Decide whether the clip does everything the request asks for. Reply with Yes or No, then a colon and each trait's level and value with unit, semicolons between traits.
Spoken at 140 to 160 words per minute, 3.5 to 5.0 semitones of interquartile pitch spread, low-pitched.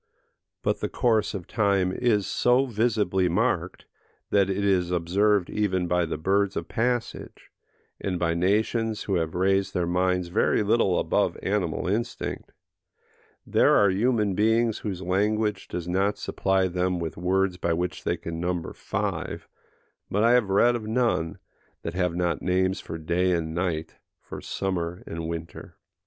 No: average, 155 wpm; average, 3.0 semitones; very low, 95 Hz